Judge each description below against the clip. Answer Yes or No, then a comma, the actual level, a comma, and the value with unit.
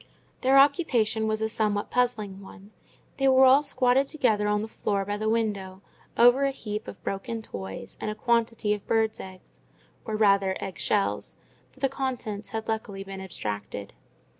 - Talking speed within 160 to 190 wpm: Yes, average, 165 wpm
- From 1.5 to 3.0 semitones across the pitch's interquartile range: No, average, 3.7 semitones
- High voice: Yes, high, 215 Hz